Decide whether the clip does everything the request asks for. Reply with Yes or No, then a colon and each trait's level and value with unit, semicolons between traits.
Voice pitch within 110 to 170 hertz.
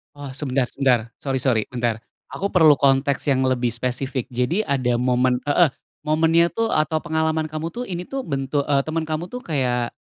Yes: medium, 140 Hz